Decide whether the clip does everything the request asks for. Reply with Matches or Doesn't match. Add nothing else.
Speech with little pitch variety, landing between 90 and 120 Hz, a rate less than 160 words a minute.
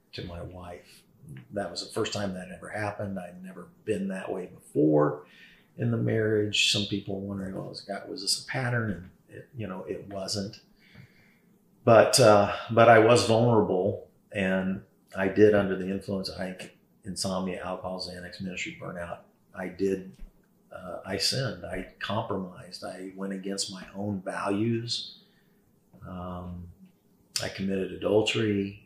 Matches